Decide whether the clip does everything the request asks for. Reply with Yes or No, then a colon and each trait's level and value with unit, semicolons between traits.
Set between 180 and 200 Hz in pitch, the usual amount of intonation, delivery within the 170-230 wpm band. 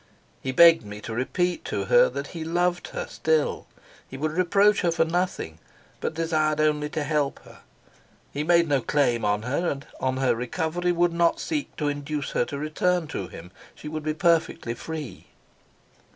No: medium, 155 Hz; average, 3.8 semitones; average, 180 wpm